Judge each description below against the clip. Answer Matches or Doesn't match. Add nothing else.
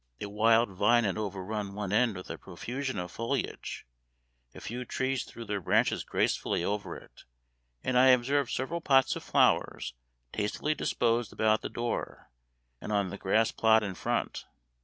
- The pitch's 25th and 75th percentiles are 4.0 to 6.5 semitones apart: Doesn't match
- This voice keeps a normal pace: Matches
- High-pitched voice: Doesn't match